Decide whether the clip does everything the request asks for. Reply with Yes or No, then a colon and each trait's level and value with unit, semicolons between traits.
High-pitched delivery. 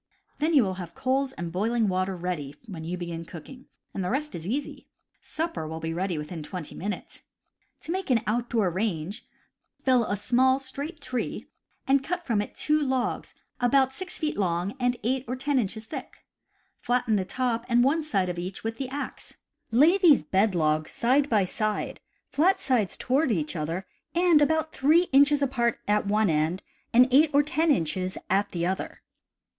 Yes: high, 235 Hz